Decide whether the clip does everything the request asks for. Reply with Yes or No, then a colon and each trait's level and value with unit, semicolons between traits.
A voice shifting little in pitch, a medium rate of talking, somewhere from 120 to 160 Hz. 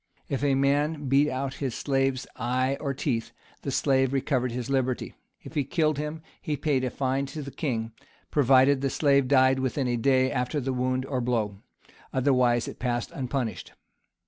Yes: narrow, 1.7 semitones; average, 175 wpm; low, 135 Hz